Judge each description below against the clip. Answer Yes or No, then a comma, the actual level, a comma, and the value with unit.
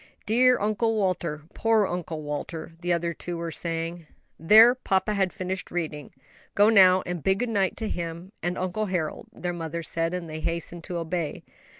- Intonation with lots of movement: No, average, 3.0 semitones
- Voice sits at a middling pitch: Yes, medium, 175 Hz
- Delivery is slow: No, average, 180 wpm